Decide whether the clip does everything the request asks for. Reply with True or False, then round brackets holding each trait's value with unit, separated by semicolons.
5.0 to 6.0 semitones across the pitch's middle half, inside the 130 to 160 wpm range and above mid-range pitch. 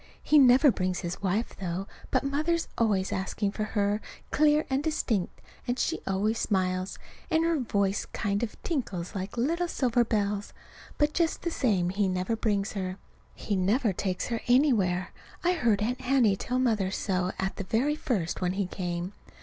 False (5.4 semitones; 175 wpm; 210 Hz)